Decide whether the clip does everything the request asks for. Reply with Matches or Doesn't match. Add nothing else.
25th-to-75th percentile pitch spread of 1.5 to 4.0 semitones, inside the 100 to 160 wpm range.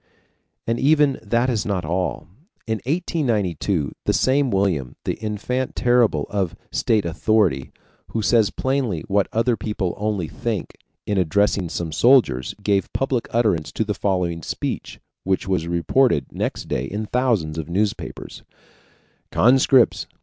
Doesn't match